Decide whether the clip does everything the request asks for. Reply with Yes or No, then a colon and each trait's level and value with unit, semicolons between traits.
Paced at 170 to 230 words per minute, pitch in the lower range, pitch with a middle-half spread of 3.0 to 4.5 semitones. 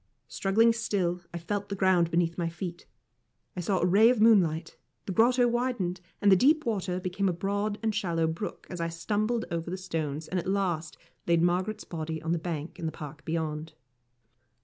No: average, 195 wpm; medium, 180 Hz; average, 3.6 semitones